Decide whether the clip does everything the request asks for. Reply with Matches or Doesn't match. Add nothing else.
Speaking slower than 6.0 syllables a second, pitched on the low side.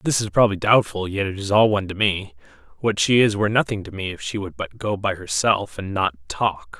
Matches